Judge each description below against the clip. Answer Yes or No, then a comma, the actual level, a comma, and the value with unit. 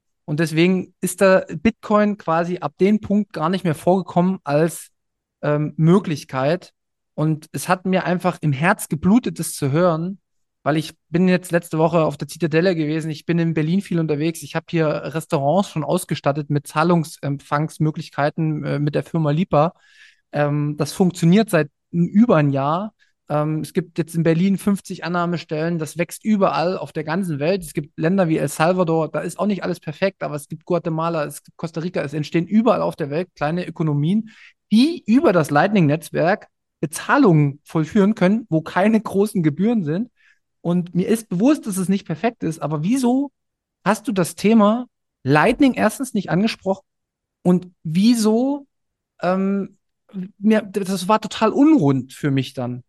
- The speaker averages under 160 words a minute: No, average, 165 wpm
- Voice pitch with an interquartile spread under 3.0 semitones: No, average, 4.0 semitones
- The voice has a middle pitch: Yes, medium, 170 Hz